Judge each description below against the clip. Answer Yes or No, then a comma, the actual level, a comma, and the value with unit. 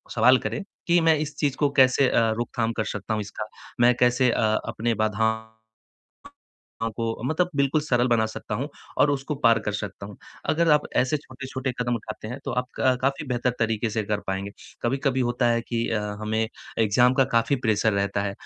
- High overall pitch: No, low, 120 Hz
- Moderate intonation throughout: Yes, average, 3.2 semitones